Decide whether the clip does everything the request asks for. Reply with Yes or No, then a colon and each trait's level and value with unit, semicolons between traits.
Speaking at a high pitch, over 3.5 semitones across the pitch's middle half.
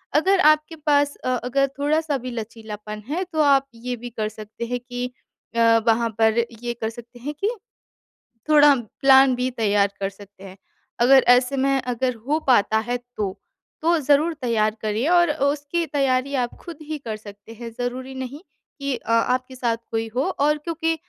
Yes: very high, 255 Hz; average, 4.1 semitones